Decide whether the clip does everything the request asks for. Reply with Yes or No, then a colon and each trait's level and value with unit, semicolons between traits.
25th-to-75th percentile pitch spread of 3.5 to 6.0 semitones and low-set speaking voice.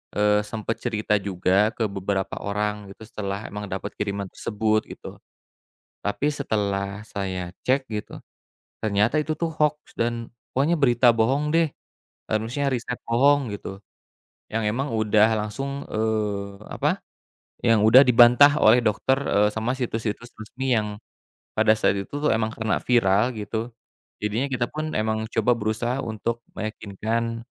No: average, 3.0 semitones; low, 110 Hz